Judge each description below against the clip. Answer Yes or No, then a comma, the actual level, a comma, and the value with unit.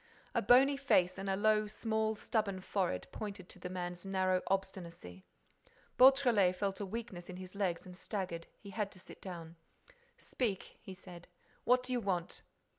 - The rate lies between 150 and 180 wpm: Yes, average, 170 wpm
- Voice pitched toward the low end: No, high, 195 Hz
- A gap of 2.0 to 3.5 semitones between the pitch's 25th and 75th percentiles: Yes, average, 3.1 semitones